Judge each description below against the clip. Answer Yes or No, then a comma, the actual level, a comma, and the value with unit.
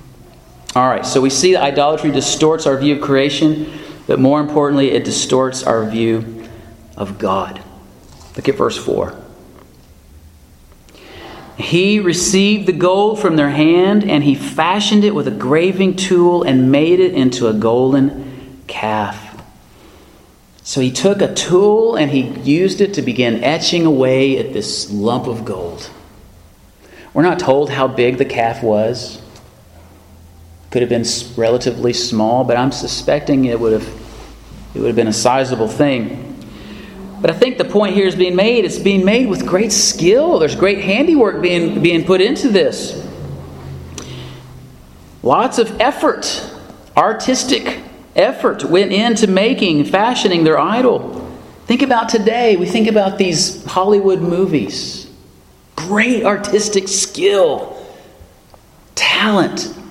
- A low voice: No, medium, 145 Hz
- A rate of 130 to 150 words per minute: Yes, average, 140 wpm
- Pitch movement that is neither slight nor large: No, wide, 8.9 semitones